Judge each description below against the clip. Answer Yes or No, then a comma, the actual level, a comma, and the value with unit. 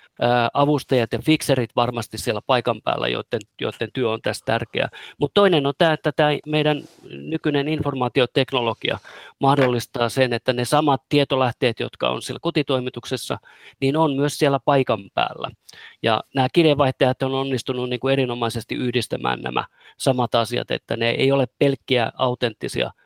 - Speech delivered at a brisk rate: No, average, 145 wpm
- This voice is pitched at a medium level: No, low, 130 Hz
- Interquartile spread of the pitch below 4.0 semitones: Yes, average, 2.8 semitones